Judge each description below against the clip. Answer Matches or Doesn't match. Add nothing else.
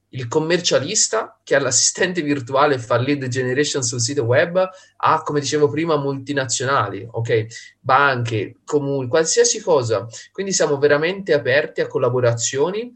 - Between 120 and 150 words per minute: Matches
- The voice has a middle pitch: Matches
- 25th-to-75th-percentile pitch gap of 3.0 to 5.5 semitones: Matches